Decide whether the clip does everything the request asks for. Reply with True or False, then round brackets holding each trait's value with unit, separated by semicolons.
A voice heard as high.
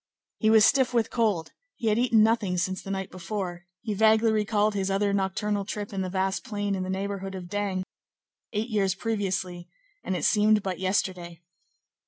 True (200 Hz)